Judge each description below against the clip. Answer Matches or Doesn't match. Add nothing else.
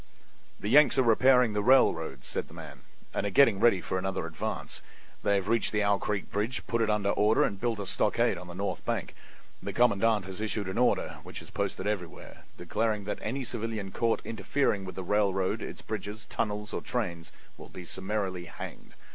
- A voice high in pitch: Doesn't match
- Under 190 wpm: Doesn't match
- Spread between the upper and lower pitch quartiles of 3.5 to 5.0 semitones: Doesn't match